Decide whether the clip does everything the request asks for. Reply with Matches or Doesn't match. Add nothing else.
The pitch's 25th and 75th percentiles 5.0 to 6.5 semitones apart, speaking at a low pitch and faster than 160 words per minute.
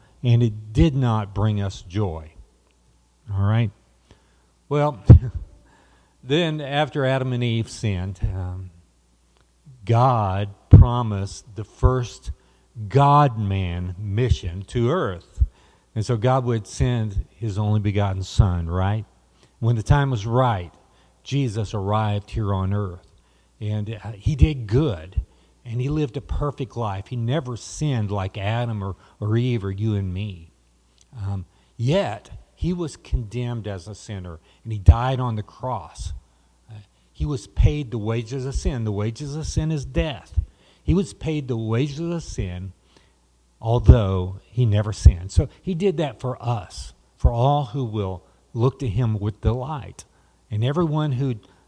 Doesn't match